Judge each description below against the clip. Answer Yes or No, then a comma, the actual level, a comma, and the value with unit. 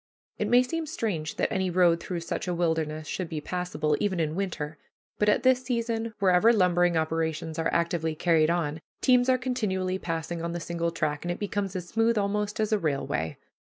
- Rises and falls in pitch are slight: No, average, 4.4 semitones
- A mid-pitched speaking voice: Yes, medium, 175 Hz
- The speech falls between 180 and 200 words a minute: Yes, average, 195 wpm